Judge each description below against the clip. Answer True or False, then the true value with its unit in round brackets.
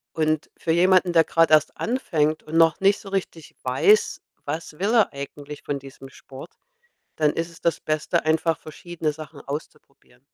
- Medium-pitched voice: True (160 Hz)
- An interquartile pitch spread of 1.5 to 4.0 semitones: True (2.6 semitones)